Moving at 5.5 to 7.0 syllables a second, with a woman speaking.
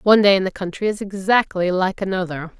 Yes: 6.1 syllables/s; female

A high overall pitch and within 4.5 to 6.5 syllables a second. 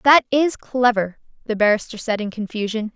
Yes: high, 225 Hz; 5.2 syllables/s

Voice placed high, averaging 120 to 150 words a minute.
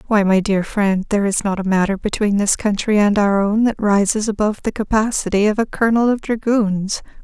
No: high, 205 Hz; fast, 205 wpm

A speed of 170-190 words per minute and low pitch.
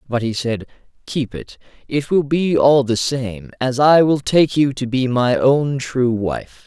No: average, 200 wpm; low, 130 Hz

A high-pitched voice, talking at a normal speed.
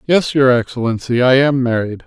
No: low, 130 Hz; average, 175 wpm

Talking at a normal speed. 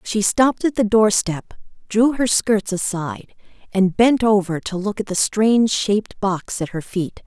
Yes: average, 180 wpm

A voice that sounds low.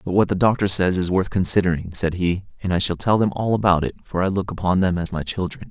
Yes: very low, 95 Hz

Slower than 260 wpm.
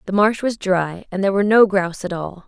No: fast, 265 wpm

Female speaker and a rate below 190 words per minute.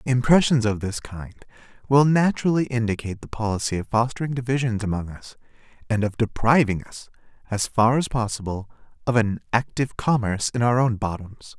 No: male; average, 155 wpm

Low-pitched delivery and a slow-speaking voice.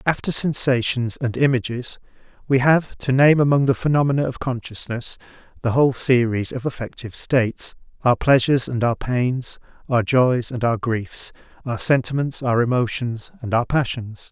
No: low, 125 Hz; average, 145 wpm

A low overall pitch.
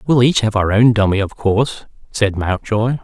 Yes: low, 110 Hz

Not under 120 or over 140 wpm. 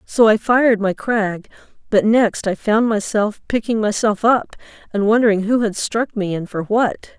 No: average, 185 wpm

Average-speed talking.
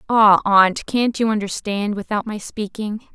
Yes: average, 155 wpm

